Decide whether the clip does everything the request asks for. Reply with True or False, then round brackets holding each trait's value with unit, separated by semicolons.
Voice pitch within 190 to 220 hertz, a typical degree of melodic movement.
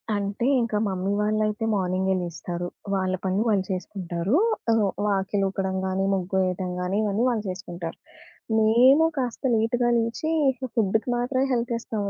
True (200 Hz; 3.3 semitones)